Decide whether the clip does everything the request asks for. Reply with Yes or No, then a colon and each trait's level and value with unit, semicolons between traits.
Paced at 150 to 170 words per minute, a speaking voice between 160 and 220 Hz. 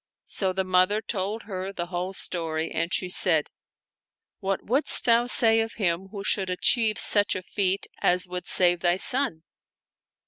Yes: average, 165 wpm; high, 190 Hz